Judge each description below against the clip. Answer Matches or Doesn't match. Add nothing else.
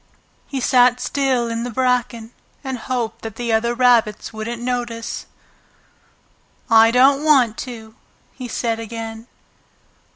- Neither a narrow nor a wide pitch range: Doesn't match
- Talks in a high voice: Matches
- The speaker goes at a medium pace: Doesn't match